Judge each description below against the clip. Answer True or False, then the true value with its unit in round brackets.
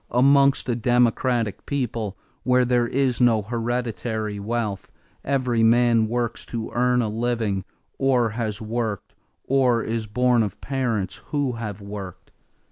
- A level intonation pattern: True (2.3 semitones)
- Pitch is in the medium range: False (120 Hz)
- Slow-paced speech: True (130 wpm)